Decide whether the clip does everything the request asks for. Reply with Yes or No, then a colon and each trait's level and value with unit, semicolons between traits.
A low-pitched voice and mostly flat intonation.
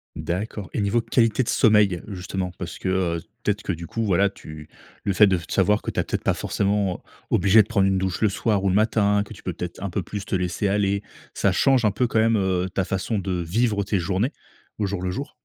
Yes: low, 100 Hz; narrow, 2.3 semitones